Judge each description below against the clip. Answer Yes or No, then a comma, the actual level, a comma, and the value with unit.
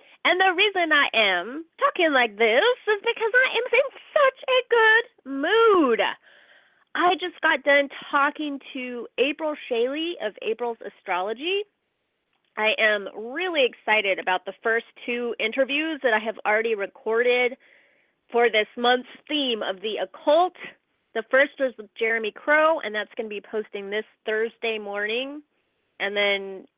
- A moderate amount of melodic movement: No, wide, 6.9 semitones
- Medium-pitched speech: No, very high, 260 Hz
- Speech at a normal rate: Yes, average, 150 wpm